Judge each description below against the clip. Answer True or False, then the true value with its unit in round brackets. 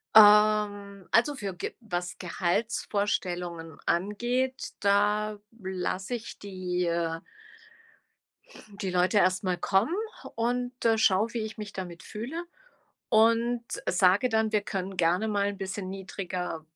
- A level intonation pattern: False (3.3 semitones)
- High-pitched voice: True (200 Hz)